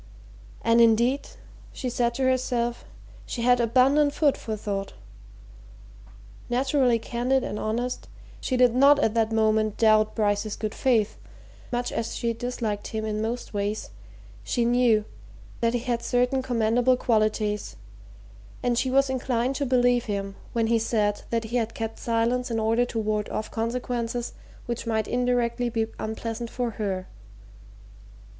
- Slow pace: No, average, 150 wpm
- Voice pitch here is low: No, high, 235 Hz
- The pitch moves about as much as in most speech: No, narrow, 2.1 semitones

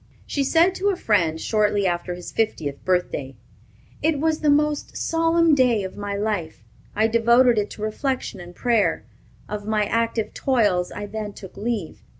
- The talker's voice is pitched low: No, high, 215 Hz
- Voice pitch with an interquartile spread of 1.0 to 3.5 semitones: No, average, 5.0 semitones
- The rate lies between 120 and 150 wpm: No, average, 165 wpm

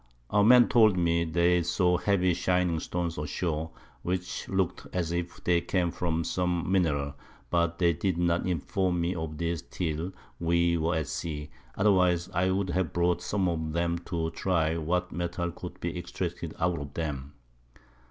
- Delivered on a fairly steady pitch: Yes, narrow, 1.6 semitones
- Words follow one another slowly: No, average, 170 wpm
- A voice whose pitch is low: Yes, very low, 85 Hz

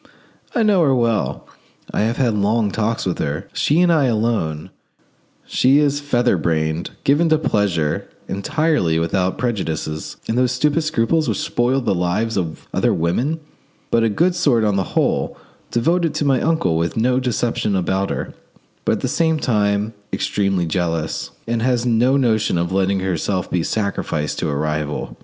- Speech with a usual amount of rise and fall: No, wide, 6.6 semitones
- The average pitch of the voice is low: Yes, low, 110 Hz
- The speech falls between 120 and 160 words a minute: No, average, 170 wpm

